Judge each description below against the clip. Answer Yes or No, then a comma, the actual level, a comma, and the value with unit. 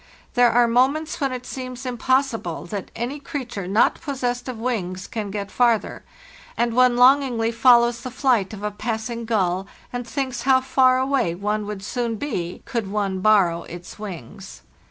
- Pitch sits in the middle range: No, high, 235 Hz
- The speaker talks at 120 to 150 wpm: No, average, 165 wpm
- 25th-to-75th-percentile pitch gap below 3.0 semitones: No, average, 3.7 semitones